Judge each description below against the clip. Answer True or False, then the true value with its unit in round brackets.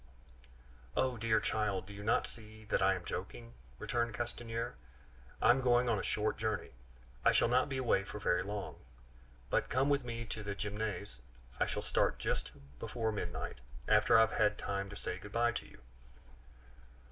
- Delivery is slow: False (180 wpm)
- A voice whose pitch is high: False (110 Hz)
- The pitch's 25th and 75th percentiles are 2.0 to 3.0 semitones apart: True (2.7 semitones)